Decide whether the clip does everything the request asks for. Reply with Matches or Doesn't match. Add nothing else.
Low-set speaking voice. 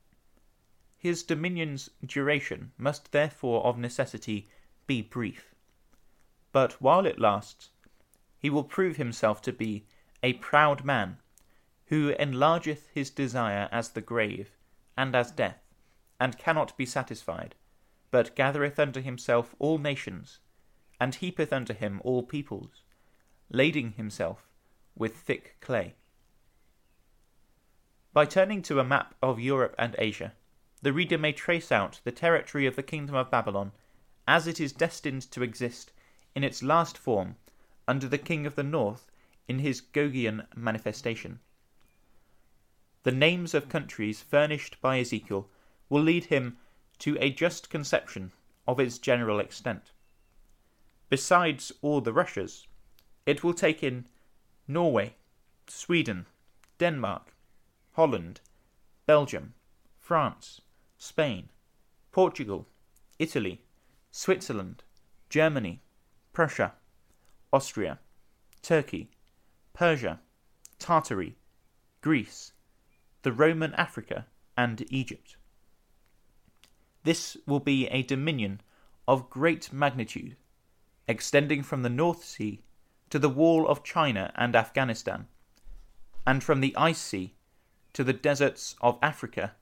Matches